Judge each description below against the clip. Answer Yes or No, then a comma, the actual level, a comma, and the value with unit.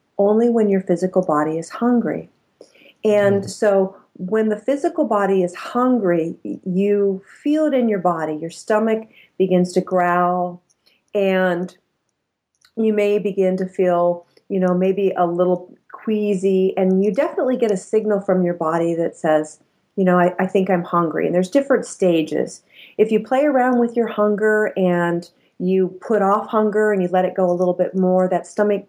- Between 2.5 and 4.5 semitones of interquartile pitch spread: Yes, average, 3.0 semitones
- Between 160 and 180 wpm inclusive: Yes, average, 170 wpm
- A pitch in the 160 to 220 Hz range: Yes, high, 190 Hz